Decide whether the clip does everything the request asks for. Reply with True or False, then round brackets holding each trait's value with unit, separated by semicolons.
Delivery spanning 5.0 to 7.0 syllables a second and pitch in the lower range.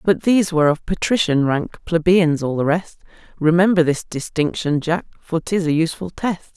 False (5.1 syllables/s; 165 Hz)